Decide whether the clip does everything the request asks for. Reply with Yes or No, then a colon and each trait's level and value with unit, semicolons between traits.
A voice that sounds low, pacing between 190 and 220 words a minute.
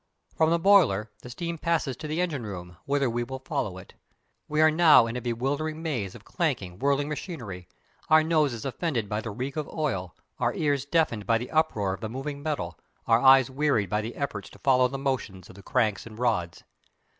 Yes: low, 130 Hz; fast, 205 wpm